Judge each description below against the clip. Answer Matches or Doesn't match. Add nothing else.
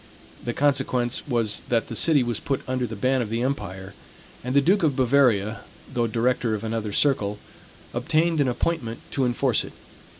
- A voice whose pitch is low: Matches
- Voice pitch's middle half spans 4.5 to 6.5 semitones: Doesn't match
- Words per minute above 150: Matches